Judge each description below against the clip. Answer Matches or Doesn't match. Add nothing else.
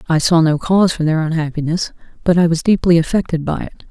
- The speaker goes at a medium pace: Doesn't match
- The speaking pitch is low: Doesn't match